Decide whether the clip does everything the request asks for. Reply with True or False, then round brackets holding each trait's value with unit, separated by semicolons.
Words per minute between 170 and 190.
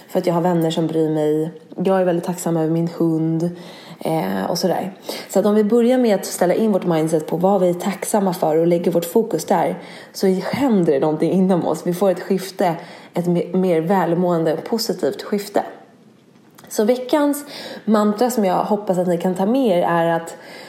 False (200 wpm)